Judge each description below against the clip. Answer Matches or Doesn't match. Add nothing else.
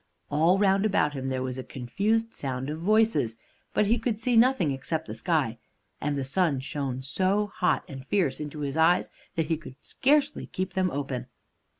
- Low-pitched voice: Doesn't match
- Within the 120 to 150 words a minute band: Doesn't match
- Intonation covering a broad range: Matches